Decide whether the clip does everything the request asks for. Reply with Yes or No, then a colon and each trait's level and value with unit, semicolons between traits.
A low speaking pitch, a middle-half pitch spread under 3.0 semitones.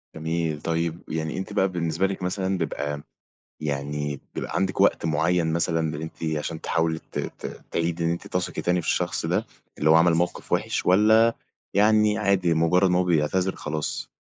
Yes: very low, 85 Hz; narrow, 2.4 semitones